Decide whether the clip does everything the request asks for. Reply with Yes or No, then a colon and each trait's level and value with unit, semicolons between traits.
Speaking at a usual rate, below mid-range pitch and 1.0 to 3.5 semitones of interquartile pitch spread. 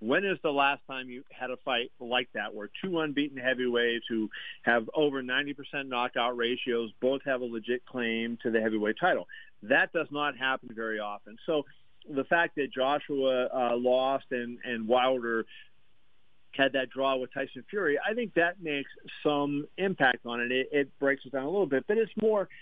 Yes: average, 190 wpm; low, 130 Hz; average, 3.1 semitones